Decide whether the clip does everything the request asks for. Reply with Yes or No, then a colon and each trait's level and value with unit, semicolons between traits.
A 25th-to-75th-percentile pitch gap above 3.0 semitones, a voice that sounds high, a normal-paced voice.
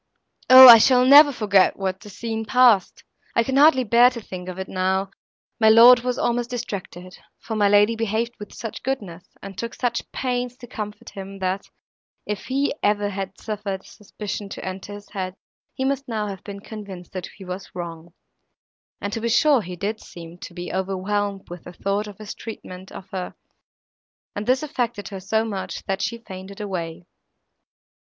Yes: average, 3.6 semitones; high, 205 Hz; average, 185 wpm